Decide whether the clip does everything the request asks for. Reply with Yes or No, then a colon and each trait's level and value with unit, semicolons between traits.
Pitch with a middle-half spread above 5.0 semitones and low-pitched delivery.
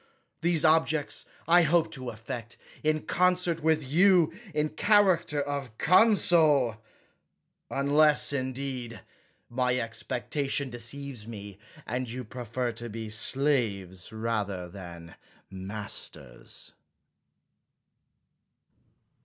Yes: wide, 5.6 semitones; low, 130 Hz